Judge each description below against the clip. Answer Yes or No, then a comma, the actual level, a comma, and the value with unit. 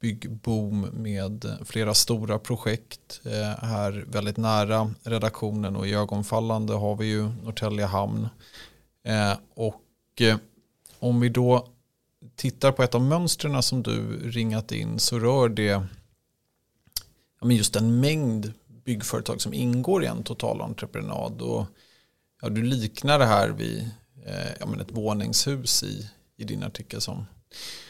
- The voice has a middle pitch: No, low, 110 Hz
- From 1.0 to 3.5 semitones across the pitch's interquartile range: Yes, narrow, 2.5 semitones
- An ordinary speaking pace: No, slow, 115 wpm